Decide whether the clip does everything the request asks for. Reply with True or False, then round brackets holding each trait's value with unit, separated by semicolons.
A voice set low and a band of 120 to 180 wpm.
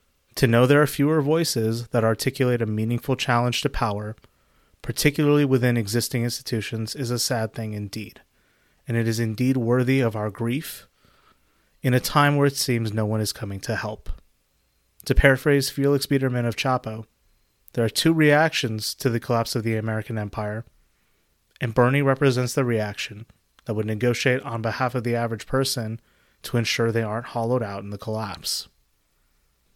True (115 Hz; 165 wpm)